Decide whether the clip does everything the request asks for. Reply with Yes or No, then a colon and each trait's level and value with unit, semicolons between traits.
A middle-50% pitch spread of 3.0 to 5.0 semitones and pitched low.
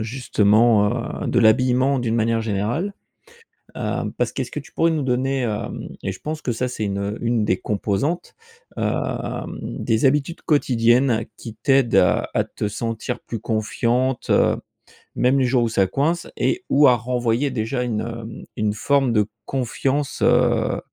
Yes: average, 3.4 semitones; low, 120 Hz